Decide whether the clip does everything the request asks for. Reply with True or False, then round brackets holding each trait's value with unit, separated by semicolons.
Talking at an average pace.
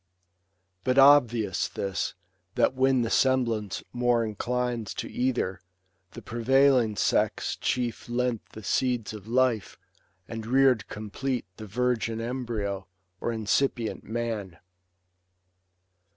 False (110 wpm)